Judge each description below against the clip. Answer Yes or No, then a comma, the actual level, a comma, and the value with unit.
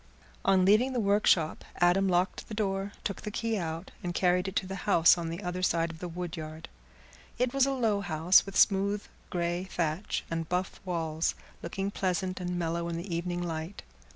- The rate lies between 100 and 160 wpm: No, average, 190 wpm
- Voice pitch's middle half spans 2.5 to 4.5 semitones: Yes, average, 2.8 semitones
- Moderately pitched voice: Yes, medium, 180 Hz